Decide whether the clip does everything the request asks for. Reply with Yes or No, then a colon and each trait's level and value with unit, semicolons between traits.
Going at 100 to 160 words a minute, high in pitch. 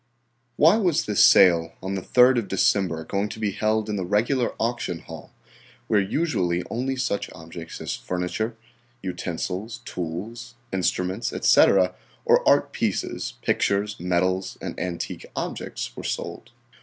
No: average, 140 wpm; low, 100 Hz